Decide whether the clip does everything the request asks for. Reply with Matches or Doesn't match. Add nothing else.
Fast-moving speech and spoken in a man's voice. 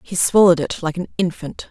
Doesn't match